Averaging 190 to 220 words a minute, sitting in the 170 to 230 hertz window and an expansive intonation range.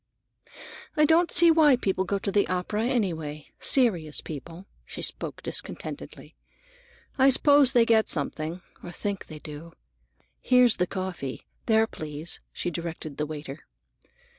No: slow, 135 wpm; medium, 185 Hz; wide, 7.5 semitones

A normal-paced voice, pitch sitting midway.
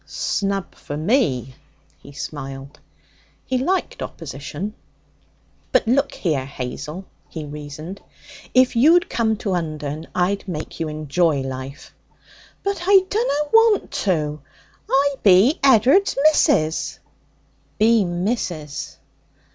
No: slow, 105 wpm; medium, 180 Hz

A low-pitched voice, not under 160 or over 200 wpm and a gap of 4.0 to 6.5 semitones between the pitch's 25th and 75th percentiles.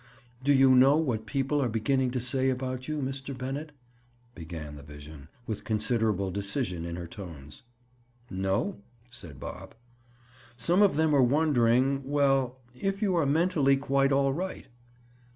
No: low, 130 Hz; average, 145 wpm; wide, 5.6 semitones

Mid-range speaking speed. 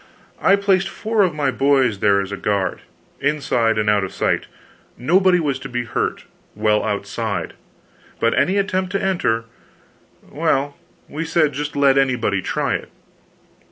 Yes: average, 155 wpm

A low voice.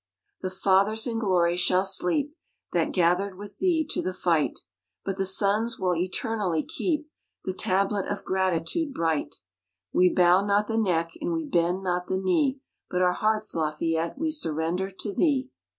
No: high, 190 Hz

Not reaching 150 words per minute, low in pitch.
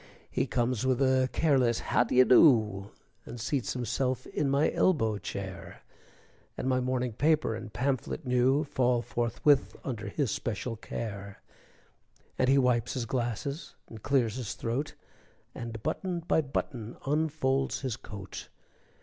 Yes: average, 140 wpm; low, 125 Hz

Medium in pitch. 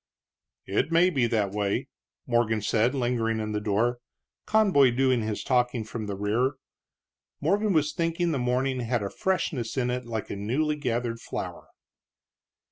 No: low, 125 Hz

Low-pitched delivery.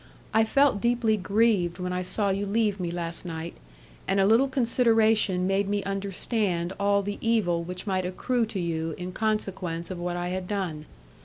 No: high, 195 Hz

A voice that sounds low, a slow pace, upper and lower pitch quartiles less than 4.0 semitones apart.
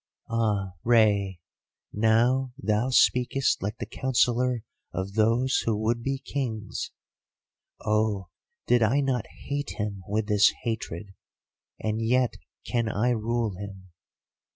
Yes: low, 110 Hz; slow, 120 wpm; average, 2.9 semitones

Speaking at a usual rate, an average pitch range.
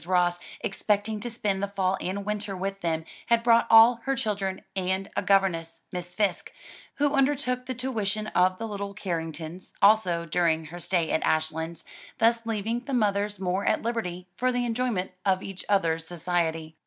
Yes: average, 170 wpm; average, 4.2 semitones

